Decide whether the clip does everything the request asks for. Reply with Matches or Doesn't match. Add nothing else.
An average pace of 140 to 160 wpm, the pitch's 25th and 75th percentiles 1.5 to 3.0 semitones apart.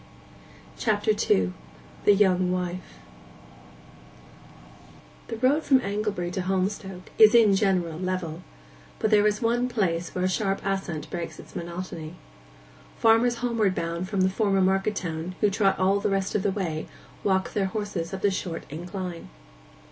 Matches